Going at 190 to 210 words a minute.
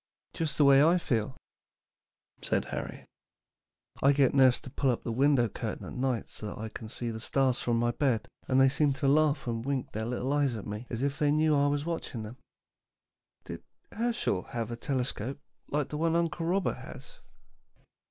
Yes: average, 195 wpm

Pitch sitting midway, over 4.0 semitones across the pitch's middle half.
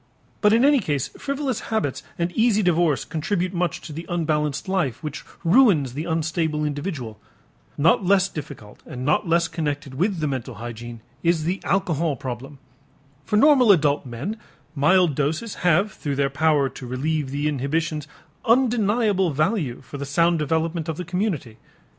Yes: medium, 160 Hz; average, 4.8 semitones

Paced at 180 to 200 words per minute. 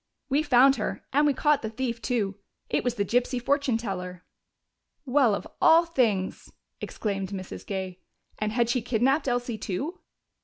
No: average, 160 wpm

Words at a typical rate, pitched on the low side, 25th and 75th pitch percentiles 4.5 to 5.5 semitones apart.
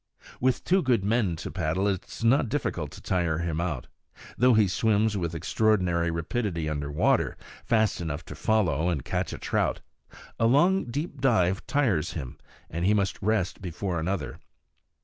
Yes: average, 170 wpm; very low, 95 Hz; average, 5.2 semitones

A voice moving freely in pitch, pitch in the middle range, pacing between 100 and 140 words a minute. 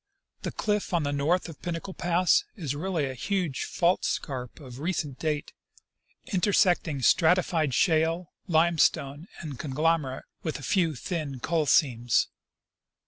No: average, 3.8 semitones; medium, 160 Hz; slow, 135 wpm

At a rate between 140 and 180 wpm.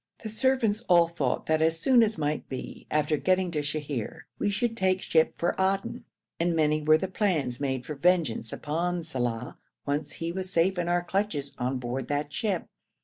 No: average, 190 wpm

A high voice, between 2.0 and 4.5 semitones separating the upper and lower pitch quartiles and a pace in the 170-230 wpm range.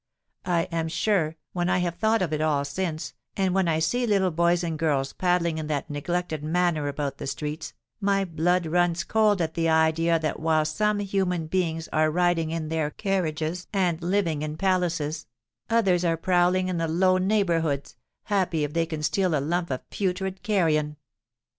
No: medium, 170 Hz; average, 2.8 semitones; average, 180 wpm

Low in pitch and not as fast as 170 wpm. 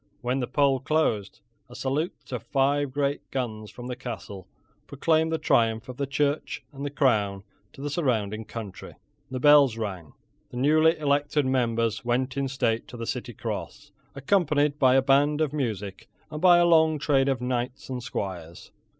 No: low, 130 Hz; average, 175 wpm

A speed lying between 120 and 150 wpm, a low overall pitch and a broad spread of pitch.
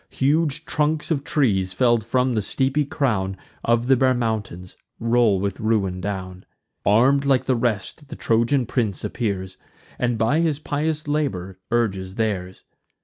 Yes: average, 145 wpm; low, 115 Hz; wide, 5.7 semitones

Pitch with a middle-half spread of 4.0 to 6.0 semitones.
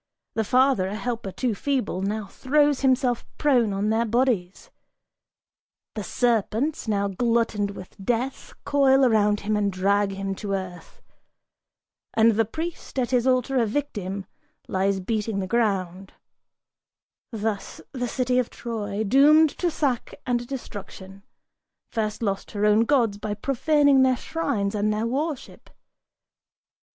Yes: average, 4.3 semitones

